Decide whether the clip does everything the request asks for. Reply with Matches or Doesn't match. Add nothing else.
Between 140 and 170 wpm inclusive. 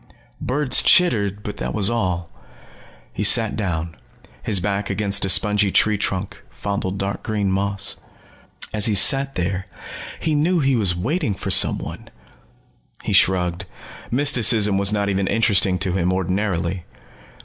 Matches